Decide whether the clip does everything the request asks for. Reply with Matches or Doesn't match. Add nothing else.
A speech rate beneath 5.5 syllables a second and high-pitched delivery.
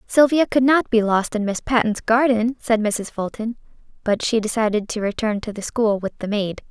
Matches